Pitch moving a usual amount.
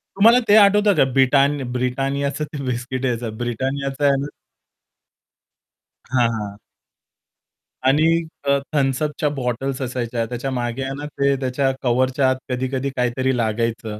No: narrow, 2.2 semitones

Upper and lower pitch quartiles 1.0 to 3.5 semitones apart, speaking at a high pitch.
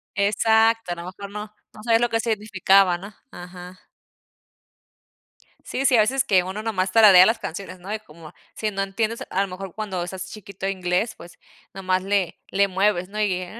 Yes: narrow, 2.6 semitones; high, 195 Hz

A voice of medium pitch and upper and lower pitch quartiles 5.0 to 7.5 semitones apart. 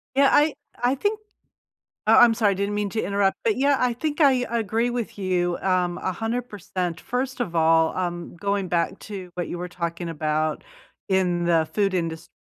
No: high, 195 Hz; wide, 5.6 semitones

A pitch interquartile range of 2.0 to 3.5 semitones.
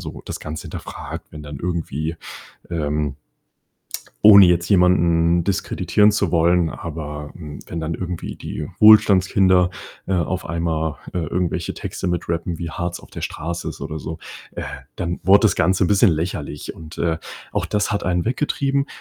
Yes: narrow, 2.6 semitones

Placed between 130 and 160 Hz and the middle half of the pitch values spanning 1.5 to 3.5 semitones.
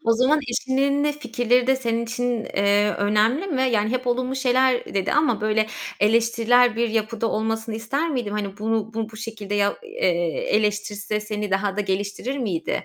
No: high, 225 Hz; average, 3.1 semitones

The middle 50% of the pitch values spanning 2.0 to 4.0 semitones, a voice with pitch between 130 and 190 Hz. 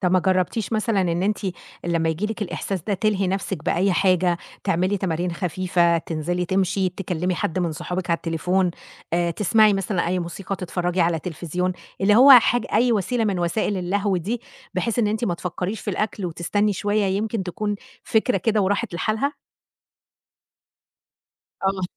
Yes: average, 3.0 semitones; medium, 185 Hz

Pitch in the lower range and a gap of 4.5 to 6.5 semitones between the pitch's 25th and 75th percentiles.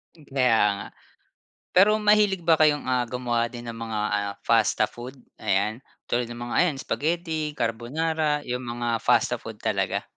Yes: low, 125 Hz; average, 5.1 semitones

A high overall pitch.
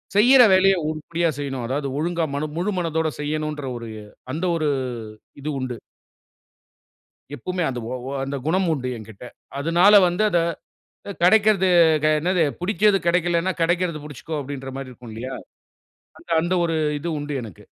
No: medium, 160 Hz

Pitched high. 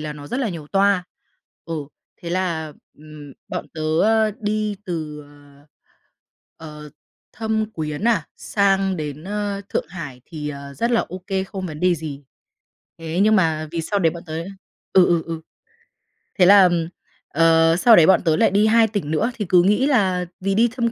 No: medium, 180 Hz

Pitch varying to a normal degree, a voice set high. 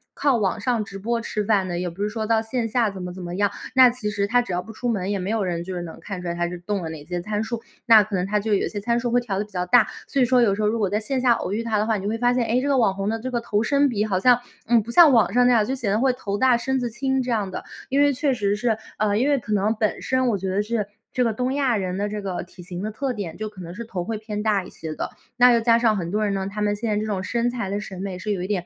Yes: average, 3.4 semitones; high, 215 Hz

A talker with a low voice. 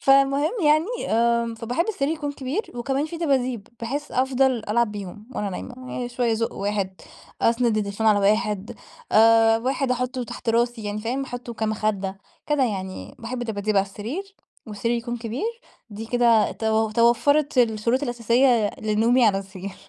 No: high, 235 Hz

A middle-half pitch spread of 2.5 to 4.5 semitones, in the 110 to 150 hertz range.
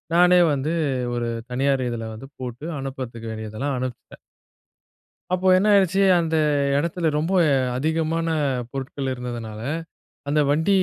No: average, 5.2 semitones; low, 135 Hz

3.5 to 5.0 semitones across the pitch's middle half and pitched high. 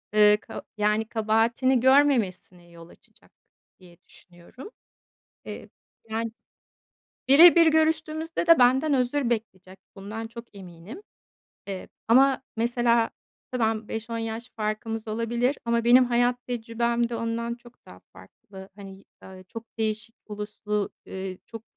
No: average, 2.8 semitones; high, 230 Hz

